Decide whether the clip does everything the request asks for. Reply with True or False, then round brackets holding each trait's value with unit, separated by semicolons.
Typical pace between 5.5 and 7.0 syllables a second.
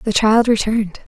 False (5.3 syllables/s)